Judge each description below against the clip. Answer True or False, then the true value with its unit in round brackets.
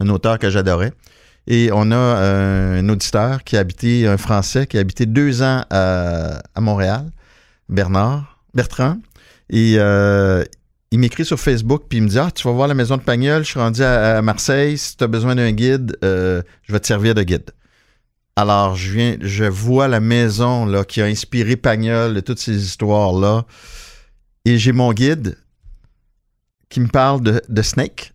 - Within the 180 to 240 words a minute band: True (190 wpm)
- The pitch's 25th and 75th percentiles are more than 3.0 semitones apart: True (3.7 semitones)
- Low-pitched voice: True (115 Hz)